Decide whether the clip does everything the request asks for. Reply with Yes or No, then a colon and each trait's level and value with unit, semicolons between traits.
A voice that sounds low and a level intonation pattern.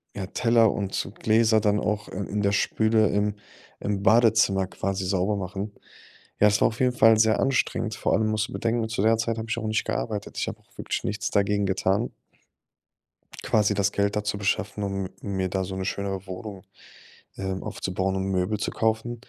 Yes: low, 105 Hz; narrow, 2.2 semitones